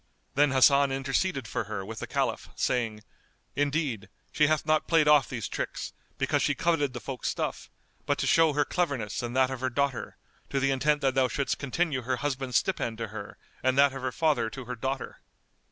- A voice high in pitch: No, low, 135 Hz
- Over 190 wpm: Yes, average, 200 wpm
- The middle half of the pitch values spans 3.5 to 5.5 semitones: No, average, 2.8 semitones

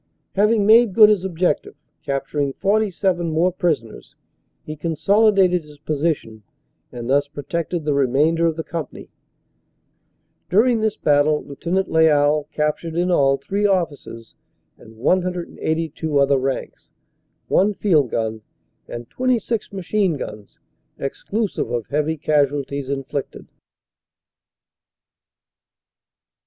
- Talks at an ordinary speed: No, slow, 105 wpm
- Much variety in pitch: No, average, 4.9 semitones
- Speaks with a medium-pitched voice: Yes, medium, 160 Hz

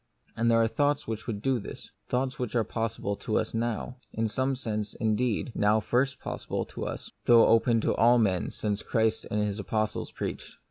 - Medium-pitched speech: No, low, 115 Hz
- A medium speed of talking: Yes, average, 195 wpm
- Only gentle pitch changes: Yes, narrow, 2.3 semitones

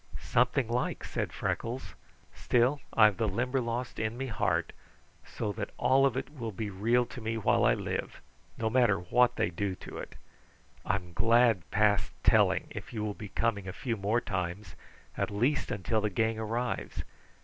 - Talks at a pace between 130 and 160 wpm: No, average, 170 wpm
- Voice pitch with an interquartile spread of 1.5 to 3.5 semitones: Yes, average, 3.1 semitones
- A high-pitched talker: No, low, 110 Hz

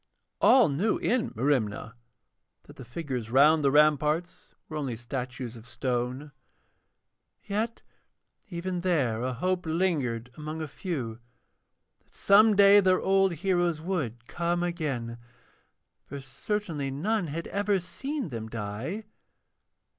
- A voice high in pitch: No, medium, 155 Hz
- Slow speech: Yes, slow, 125 wpm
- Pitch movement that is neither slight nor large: No, wide, 6.8 semitones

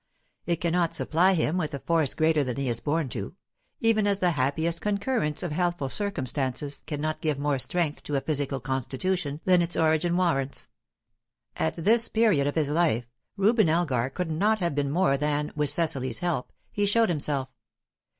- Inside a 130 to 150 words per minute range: No, average, 175 wpm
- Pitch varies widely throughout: No, average, 4.0 semitones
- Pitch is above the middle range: No, medium, 160 Hz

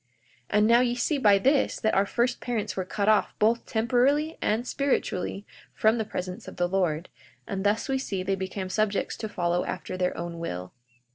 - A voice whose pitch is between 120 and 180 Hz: No, high, 210 Hz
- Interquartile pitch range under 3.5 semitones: No, average, 4.4 semitones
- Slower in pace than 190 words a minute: No, average, 200 wpm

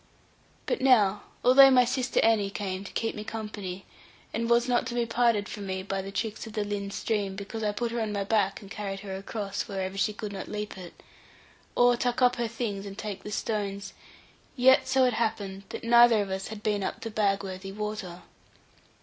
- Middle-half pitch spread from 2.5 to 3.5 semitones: Yes, average, 2.8 semitones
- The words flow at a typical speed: No, fast, 210 wpm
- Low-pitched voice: No, high, 210 Hz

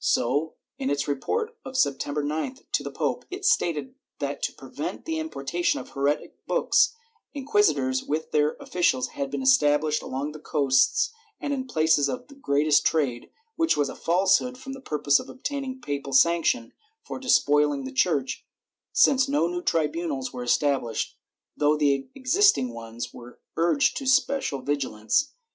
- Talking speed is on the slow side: No, average, 160 wpm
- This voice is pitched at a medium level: Yes, medium, 150 Hz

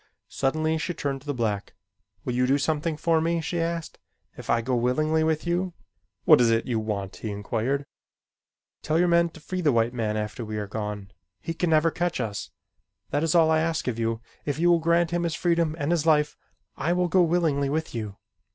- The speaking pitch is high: No, medium, 155 Hz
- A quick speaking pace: Yes, fast, 215 wpm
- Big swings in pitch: Yes, wide, 6.0 semitones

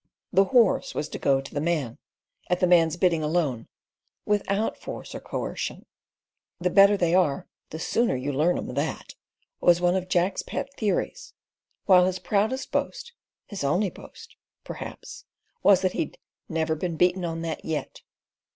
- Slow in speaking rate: No, average, 155 wpm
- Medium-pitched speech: Yes, medium, 180 Hz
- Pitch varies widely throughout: No, average, 3.8 semitones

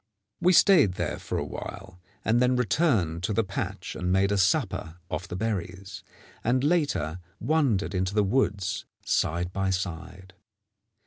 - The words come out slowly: No, average, 150 wpm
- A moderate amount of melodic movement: Yes, average, 4.1 semitones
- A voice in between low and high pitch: No, very low, 95 Hz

